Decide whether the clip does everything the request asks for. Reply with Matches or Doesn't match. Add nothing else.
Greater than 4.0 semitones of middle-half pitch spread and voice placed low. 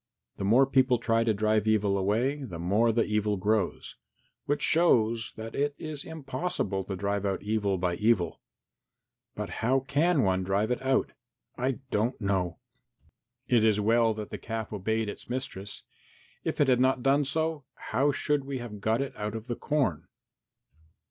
Matches